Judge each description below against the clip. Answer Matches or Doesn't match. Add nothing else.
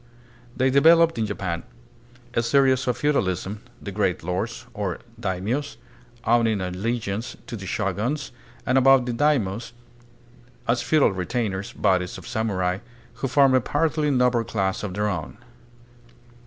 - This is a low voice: Matches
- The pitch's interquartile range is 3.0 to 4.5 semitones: Doesn't match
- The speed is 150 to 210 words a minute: Doesn't match